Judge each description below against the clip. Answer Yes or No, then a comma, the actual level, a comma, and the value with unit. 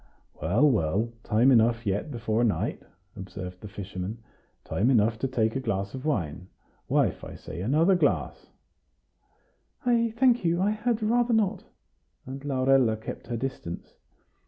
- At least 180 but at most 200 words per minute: No, average, 145 wpm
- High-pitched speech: No, low, 120 Hz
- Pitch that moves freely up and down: Yes, wide, 7.1 semitones